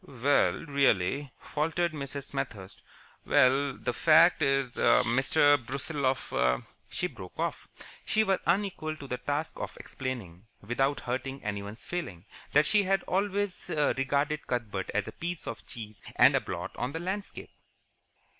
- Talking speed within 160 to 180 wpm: No, average, 145 wpm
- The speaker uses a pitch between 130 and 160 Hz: Yes, medium, 140 Hz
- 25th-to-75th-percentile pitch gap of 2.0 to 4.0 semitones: No, average, 4.6 semitones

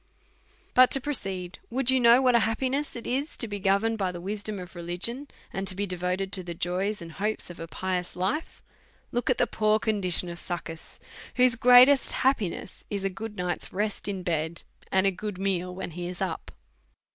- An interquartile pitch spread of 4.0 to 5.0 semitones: Yes, average, 4.5 semitones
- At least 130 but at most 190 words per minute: No, average, 200 wpm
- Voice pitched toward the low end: No, high, 195 Hz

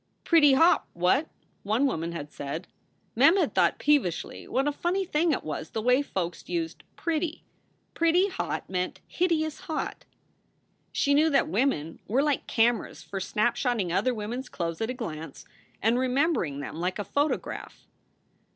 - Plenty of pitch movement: Yes, wide, 8.9 semitones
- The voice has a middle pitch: No, very high, 250 Hz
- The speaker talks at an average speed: Yes, average, 160 wpm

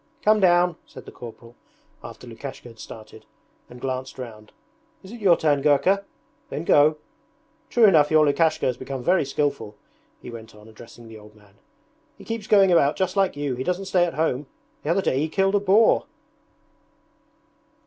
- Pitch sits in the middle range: Yes, medium, 150 Hz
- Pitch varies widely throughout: Yes, wide, 7.4 semitones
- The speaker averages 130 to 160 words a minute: No, average, 180 wpm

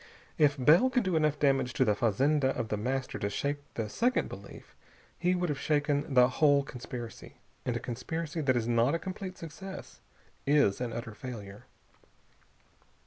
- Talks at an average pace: Yes, average, 170 wpm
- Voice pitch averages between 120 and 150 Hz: Yes, low, 135 Hz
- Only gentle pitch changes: No, average, 4.5 semitones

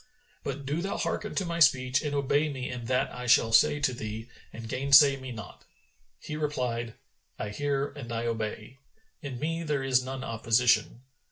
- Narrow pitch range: No, average, 3.5 semitones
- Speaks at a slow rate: No, average, 180 wpm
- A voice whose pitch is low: Yes, low, 130 Hz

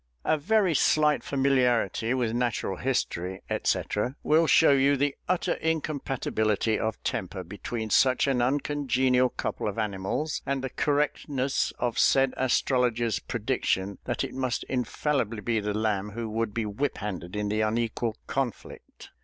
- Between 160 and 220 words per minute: No, average, 140 wpm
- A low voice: Yes, low, 125 Hz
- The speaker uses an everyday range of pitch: Yes, average, 4.1 semitones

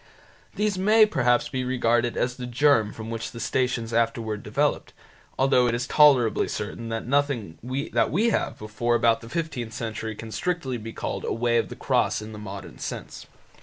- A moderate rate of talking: Yes, average, 185 wpm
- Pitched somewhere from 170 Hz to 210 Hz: No, low, 120 Hz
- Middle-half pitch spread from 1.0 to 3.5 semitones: Yes, average, 2.8 semitones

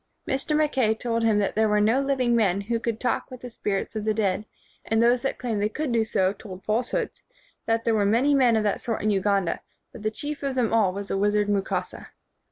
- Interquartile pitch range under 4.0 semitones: Yes, average, 3.1 semitones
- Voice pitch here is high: Yes, high, 220 Hz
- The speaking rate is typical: No, fast, 240 wpm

